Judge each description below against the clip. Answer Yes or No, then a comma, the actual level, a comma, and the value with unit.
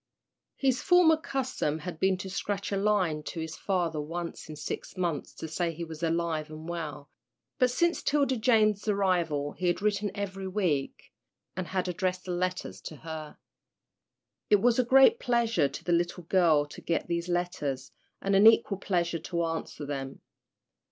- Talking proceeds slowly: No, average, 170 wpm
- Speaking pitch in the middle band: Yes, medium, 180 Hz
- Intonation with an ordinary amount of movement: Yes, average, 4.1 semitones